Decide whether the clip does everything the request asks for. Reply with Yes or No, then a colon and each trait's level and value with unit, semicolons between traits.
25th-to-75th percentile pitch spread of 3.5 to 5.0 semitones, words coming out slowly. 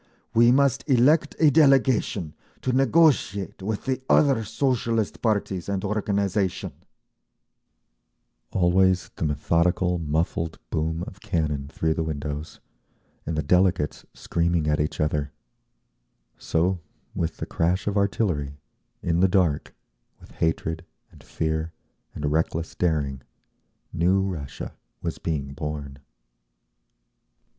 Yes: average, 4.7 semitones; slow, 115 wpm